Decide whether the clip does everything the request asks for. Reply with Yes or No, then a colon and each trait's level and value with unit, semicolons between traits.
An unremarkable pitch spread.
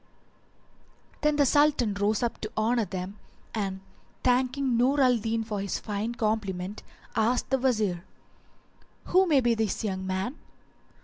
Yes: average, 3.9 semitones